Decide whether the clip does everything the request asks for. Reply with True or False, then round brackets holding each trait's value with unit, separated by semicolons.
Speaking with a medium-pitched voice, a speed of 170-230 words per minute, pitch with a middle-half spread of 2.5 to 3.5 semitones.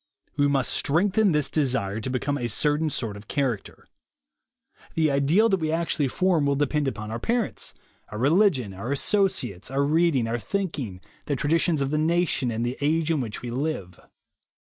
False (145 Hz; 180 wpm; 5.0 semitones)